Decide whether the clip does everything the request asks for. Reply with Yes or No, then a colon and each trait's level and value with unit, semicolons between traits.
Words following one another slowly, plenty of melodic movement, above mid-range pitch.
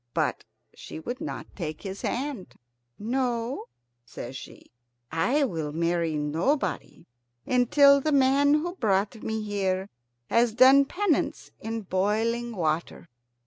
Yes: slow, 120 wpm; wide, 7.1 semitones; high, 225 Hz